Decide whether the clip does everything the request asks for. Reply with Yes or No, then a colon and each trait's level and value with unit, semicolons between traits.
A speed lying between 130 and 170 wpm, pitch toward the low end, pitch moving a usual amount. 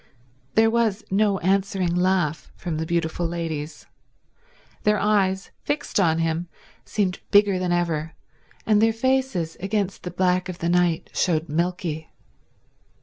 No: slow, 135 wpm; medium, 180 Hz; average, 3.4 semitones